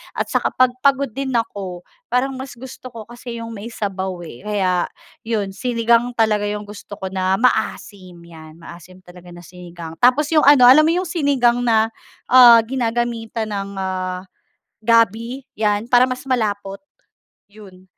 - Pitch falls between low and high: No, high, 220 Hz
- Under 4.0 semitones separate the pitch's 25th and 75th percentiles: No, average, 4.6 semitones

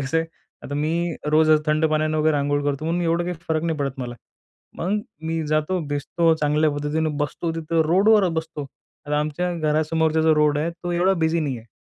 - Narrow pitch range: Yes, narrow, 1.9 semitones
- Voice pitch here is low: No, medium, 155 Hz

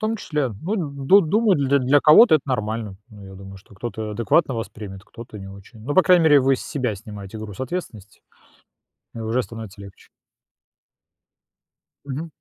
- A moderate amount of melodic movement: No, wide, 6.1 semitones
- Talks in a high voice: No, low, 115 Hz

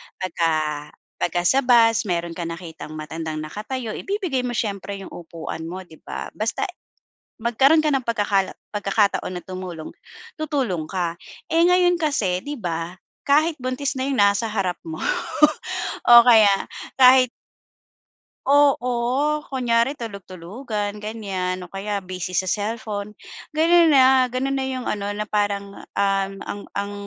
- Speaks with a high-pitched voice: Yes, high, 210 Hz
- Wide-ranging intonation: Yes, wide, 5.9 semitones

